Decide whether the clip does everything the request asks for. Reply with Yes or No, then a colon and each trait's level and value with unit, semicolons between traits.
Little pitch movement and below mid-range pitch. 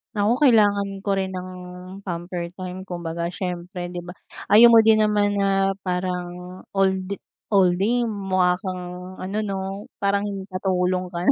No: narrow, 2.0 semitones; high, 190 Hz